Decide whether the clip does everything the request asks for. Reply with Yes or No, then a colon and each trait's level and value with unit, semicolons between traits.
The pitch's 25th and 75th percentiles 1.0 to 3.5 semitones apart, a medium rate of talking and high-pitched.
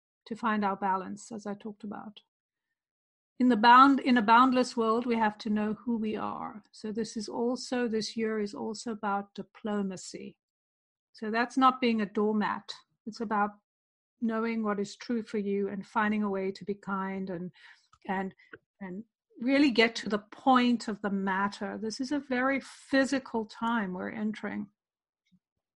Yes: average, 2.8 semitones; average, 170 wpm; high, 220 Hz